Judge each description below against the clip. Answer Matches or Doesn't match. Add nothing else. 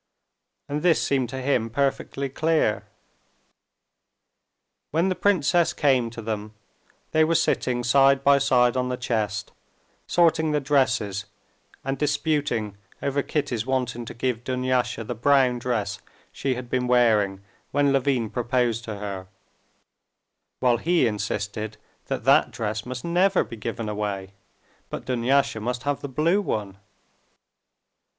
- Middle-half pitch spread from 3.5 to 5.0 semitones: Matches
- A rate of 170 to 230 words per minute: Doesn't match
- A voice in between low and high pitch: Doesn't match